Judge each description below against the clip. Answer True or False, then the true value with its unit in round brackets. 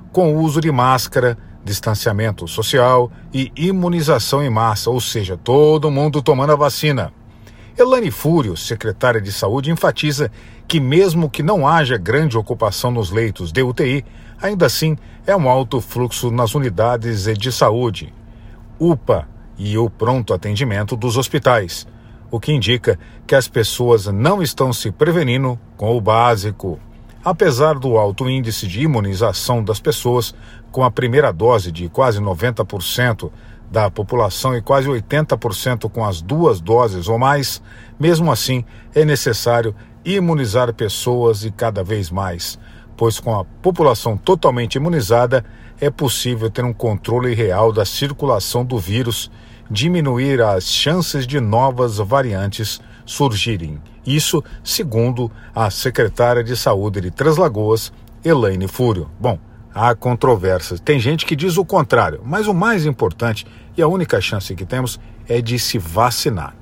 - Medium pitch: False (120 Hz)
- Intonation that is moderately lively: True (4.0 semitones)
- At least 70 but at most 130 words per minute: False (140 wpm)